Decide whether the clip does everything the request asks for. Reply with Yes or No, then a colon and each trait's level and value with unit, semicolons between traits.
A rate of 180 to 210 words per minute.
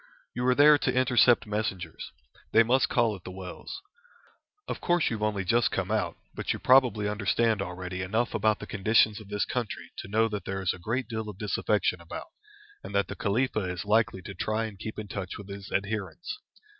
Yes: fast, 205 wpm